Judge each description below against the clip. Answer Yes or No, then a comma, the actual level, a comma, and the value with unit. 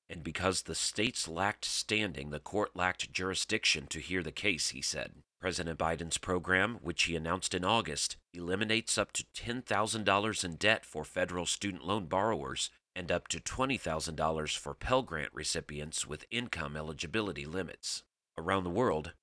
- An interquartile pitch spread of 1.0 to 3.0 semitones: No, average, 4.7 semitones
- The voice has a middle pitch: No, very low, 90 Hz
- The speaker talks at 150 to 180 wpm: Yes, average, 155 wpm